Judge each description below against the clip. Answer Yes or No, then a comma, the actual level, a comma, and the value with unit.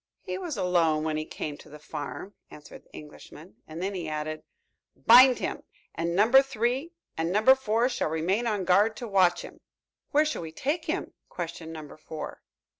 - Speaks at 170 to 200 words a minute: Yes, average, 185 wpm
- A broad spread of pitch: Yes, wide, 7.2 semitones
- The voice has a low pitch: No, medium, 185 Hz